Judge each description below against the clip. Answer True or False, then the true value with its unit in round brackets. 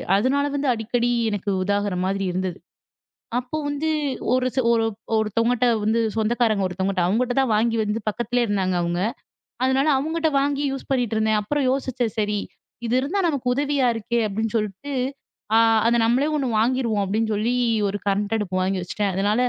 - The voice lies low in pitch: False (225 Hz)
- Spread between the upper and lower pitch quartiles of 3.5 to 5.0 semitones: True (4.0 semitones)